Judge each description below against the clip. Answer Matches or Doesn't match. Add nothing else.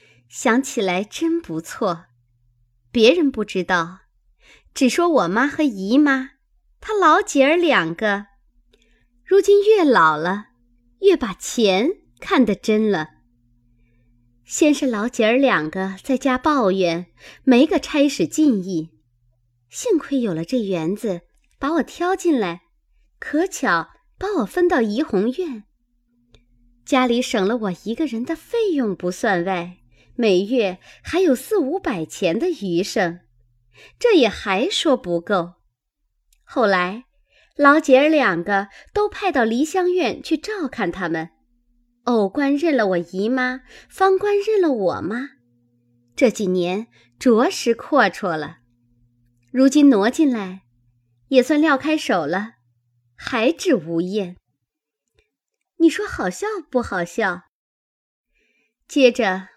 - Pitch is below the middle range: Doesn't match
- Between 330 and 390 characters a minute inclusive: Doesn't match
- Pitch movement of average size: Doesn't match